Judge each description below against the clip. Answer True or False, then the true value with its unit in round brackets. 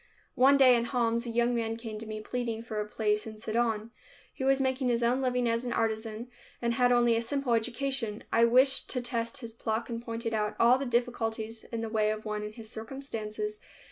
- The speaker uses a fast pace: True (220 wpm)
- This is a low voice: False (230 Hz)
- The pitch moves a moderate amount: False (1.9 semitones)